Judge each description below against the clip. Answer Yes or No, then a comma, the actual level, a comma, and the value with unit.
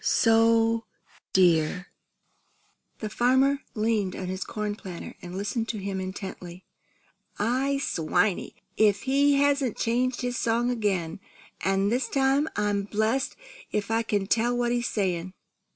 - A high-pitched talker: Yes, high, 220 Hz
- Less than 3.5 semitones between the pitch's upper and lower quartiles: No, average, 4.0 semitones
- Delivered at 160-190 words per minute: No, slow, 135 wpm